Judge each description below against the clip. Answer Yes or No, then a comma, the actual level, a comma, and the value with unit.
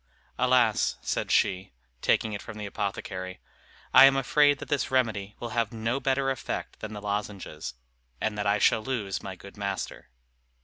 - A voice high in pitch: No, low, 105 Hz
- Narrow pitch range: No, average, 4.2 semitones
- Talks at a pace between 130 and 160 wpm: No, average, 170 wpm